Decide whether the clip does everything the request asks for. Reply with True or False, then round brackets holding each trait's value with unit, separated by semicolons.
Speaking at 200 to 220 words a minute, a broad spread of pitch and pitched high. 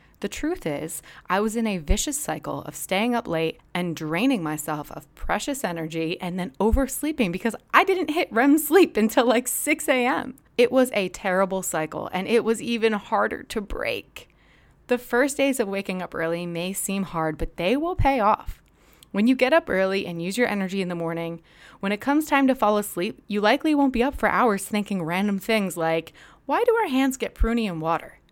True (205 wpm; 6.4 semitones; 215 Hz)